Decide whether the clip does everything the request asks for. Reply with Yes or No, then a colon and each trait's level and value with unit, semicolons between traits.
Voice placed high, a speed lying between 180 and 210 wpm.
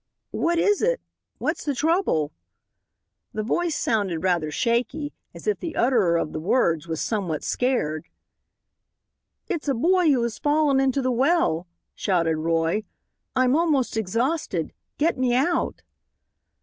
No: very high, 250 Hz; average, 140 wpm